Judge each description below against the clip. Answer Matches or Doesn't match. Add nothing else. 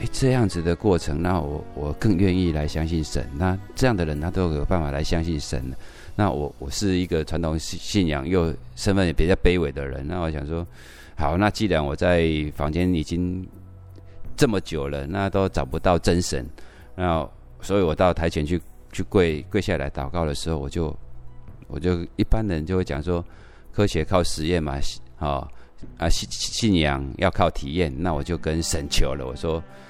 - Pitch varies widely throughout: Doesn't match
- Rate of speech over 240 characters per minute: Matches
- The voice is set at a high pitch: Doesn't match